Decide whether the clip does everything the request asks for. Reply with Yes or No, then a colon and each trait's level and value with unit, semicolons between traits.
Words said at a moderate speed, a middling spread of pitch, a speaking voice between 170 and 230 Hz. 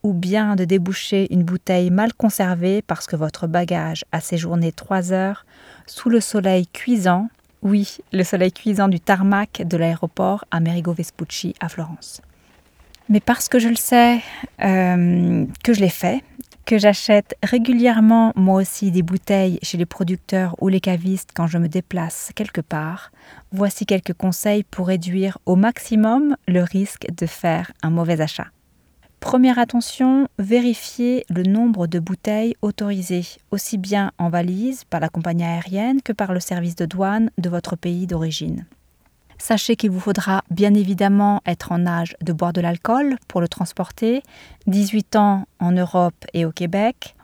Yes: average, 160 wpm; average, 3.4 semitones; high, 190 Hz